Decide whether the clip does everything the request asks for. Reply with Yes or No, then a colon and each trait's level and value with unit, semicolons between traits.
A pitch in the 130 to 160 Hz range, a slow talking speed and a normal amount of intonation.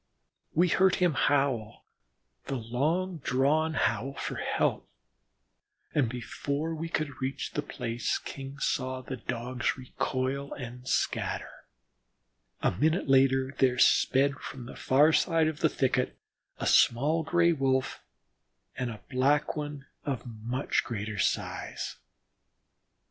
Yes: low, 135 Hz; slow, 125 wpm; average, 3.2 semitones